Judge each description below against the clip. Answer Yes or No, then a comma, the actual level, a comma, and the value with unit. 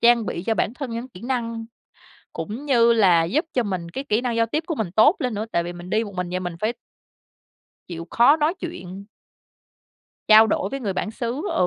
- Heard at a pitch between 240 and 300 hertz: No, high, 225 Hz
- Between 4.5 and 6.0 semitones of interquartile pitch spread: Yes, average, 5.2 semitones